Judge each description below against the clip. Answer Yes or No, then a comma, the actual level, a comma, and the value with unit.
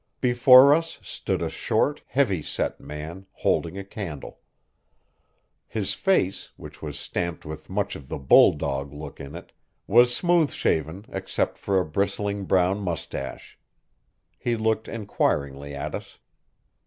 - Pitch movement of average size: No, wide, 6.6 semitones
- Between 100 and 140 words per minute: Yes, slow, 135 wpm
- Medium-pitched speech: No, very low, 95 Hz